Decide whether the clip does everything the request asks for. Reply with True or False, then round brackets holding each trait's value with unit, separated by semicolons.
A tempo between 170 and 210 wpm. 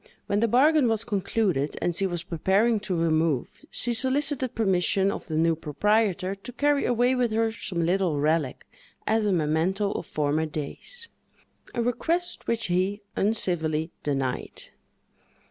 False (145 wpm)